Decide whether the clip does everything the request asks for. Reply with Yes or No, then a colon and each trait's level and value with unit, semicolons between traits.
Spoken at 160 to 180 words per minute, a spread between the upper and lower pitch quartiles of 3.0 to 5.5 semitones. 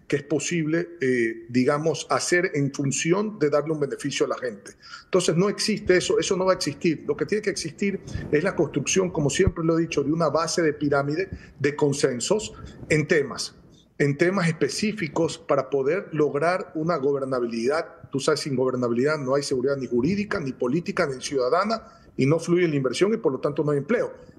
No: average, 195 wpm; average, 4.0 semitones